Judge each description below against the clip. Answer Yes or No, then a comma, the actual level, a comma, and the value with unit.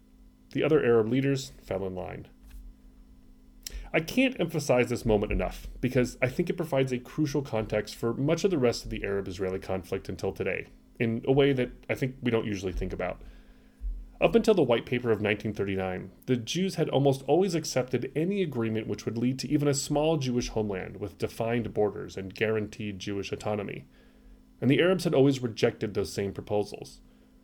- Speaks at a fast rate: No, average, 185 wpm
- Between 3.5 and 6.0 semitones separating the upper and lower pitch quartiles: Yes, wide, 5.5 semitones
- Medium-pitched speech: No, low, 115 Hz